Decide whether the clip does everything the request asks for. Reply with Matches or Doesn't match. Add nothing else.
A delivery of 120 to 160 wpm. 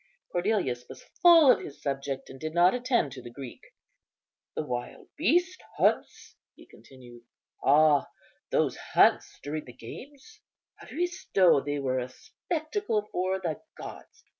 Matches